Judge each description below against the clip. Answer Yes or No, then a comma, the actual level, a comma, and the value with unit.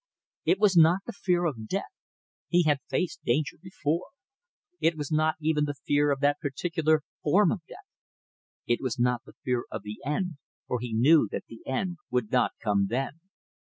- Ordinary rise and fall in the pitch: Yes, average, 5.0 semitones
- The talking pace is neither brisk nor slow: Yes, average, 185 wpm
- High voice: No, medium, 150 Hz